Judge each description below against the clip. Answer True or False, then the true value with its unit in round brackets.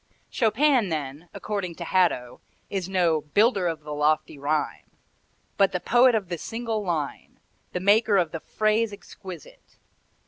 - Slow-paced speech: False (145 wpm)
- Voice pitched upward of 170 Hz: True (185 Hz)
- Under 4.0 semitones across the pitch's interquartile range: False (5.4 semitones)